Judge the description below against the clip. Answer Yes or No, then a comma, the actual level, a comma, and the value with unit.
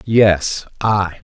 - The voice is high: No, low, 100 Hz